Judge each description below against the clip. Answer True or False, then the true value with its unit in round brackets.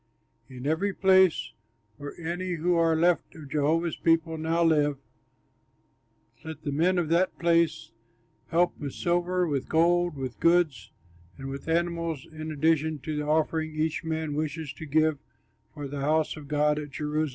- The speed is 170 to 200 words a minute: False (160 wpm)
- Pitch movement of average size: False (2.2 semitones)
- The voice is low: False (160 Hz)